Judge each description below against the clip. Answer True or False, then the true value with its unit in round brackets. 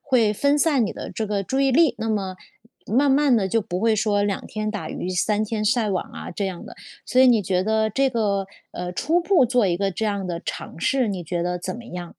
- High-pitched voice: True (215 Hz)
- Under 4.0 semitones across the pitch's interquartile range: False (4.6 semitones)